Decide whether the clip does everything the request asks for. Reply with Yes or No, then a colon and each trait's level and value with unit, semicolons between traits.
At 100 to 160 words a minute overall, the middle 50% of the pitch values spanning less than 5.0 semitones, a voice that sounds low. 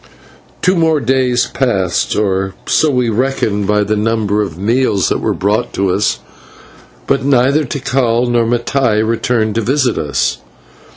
Yes: average, 150 wpm; average, 4.0 semitones; low, 115 Hz